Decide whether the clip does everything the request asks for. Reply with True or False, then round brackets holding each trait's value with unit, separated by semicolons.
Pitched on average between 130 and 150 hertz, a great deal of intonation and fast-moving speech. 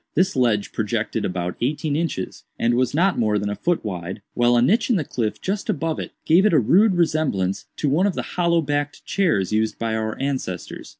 True (135 Hz; 7.8 semitones; 215 wpm)